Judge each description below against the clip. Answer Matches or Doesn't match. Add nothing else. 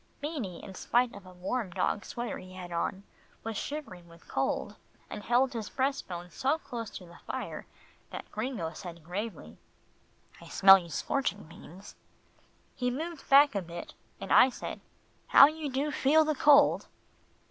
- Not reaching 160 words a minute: Doesn't match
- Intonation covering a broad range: Matches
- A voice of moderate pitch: Doesn't match